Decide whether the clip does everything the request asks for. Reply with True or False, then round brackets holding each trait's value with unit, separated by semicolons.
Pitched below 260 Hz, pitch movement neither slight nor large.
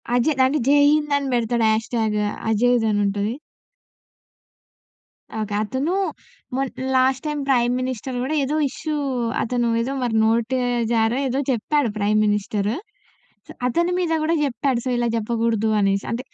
True (240 Hz; 3.3 semitones)